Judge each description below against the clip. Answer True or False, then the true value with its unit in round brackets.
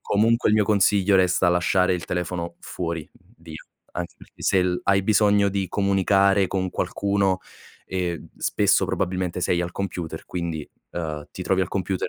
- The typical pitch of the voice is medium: False (95 Hz)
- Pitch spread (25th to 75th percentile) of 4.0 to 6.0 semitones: False (2.1 semitones)